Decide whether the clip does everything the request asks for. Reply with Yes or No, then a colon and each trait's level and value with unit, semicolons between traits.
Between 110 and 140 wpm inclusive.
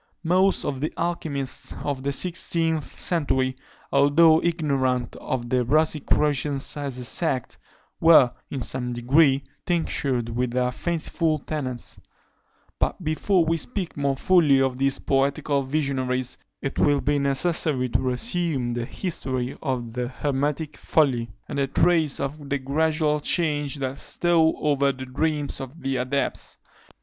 Yes: slow, 135 wpm